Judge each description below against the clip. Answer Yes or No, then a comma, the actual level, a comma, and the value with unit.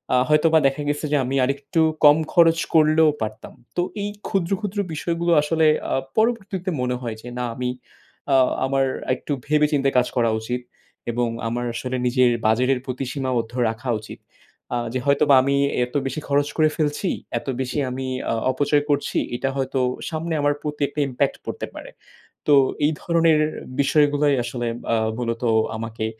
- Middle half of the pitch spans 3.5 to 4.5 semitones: Yes, average, 3.8 semitones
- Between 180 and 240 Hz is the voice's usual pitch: No, medium, 140 Hz